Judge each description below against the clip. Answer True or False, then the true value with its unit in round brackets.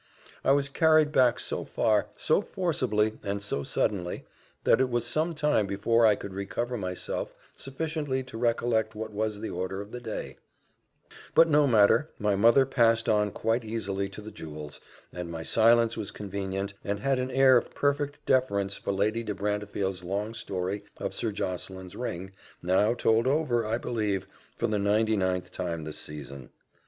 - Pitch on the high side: False (110 Hz)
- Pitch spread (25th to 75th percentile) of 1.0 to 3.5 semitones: False (4.0 semitones)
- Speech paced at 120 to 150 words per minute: False (170 wpm)